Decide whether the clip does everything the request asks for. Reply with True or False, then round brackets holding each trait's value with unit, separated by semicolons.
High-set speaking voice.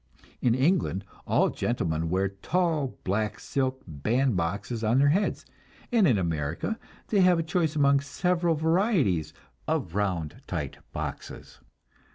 False (130 Hz)